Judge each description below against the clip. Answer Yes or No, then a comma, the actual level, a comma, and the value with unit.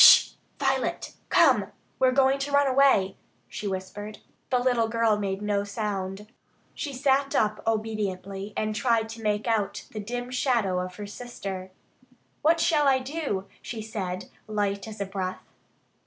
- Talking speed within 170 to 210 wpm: No, average, 155 wpm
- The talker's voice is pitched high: Yes, high, 215 Hz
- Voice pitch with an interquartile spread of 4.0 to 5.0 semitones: Yes, average, 4.3 semitones